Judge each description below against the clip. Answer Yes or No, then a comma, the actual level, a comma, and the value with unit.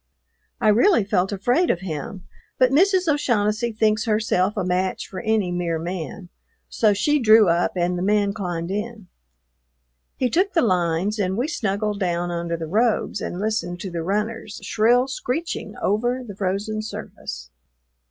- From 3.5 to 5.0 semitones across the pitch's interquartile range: Yes, average, 4.1 semitones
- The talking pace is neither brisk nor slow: Yes, average, 160 wpm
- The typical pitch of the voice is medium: No, high, 205 Hz